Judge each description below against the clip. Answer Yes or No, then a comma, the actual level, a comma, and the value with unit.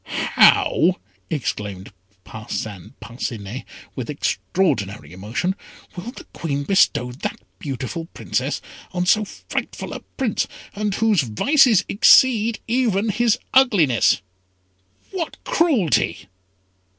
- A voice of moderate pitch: Yes, medium, 180 Hz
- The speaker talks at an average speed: No, slow, 100 wpm